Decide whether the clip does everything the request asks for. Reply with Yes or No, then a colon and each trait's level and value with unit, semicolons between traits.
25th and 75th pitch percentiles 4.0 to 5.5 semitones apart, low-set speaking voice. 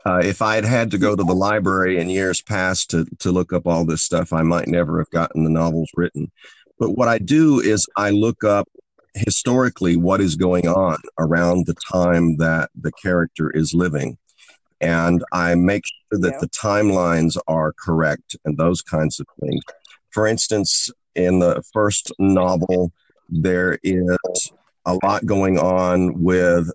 No: narrow, 2.4 semitones; very low, 90 Hz